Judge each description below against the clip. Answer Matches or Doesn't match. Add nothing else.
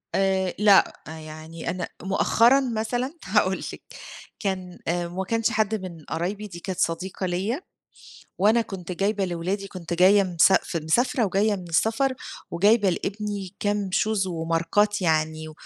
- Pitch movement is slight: Doesn't match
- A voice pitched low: Doesn't match